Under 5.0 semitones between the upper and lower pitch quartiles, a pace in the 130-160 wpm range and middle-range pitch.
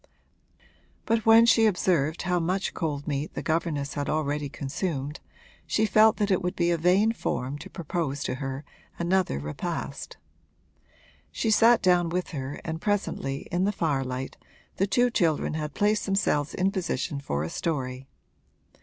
No: wide, 5.4 semitones; average, 155 wpm; medium, 165 Hz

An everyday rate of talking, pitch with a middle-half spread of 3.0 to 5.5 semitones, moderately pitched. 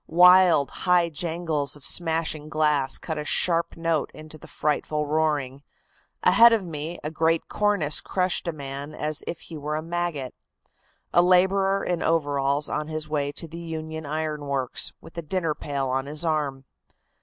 No: average, 165 wpm; narrow, 2.5 semitones; medium, 155 Hz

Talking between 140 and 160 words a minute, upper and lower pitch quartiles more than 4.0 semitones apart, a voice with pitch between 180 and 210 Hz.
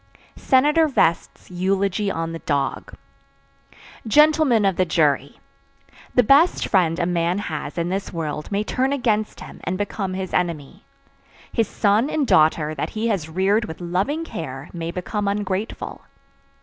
Yes: average, 150 wpm; average, 4.8 semitones; high, 190 Hz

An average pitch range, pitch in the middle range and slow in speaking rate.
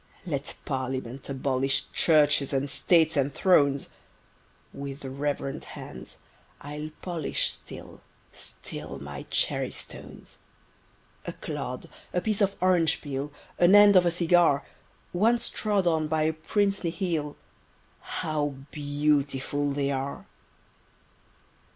Yes: average, 3.9 semitones; medium, 150 Hz; slow, 110 wpm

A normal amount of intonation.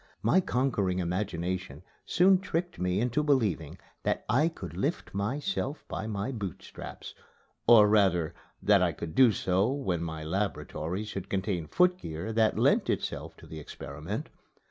No: wide, 6.6 semitones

